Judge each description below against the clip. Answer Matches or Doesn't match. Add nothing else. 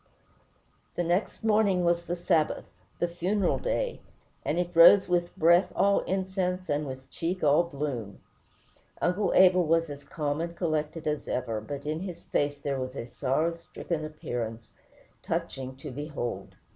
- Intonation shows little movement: Doesn't match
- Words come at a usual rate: Matches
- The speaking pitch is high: Doesn't match